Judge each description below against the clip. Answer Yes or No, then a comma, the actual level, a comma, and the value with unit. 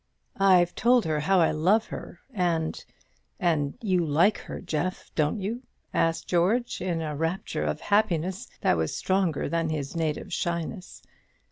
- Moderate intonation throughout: Yes, average, 3.2 semitones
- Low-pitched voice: No, medium, 175 Hz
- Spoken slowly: No, average, 150 wpm